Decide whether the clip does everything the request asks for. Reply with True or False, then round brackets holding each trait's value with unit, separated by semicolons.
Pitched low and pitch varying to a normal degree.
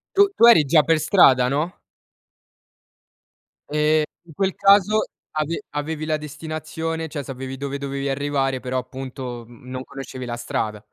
False (145 Hz; 3.5 semitones)